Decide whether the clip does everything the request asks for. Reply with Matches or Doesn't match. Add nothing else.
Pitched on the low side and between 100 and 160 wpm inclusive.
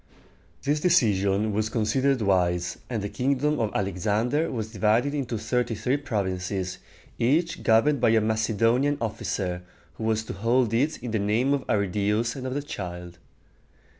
Matches